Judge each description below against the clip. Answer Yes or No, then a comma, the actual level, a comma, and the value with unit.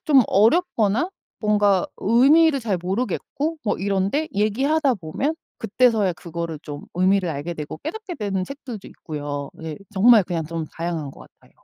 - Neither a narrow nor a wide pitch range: No, wide, 7.5 semitones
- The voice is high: Yes, high, 200 Hz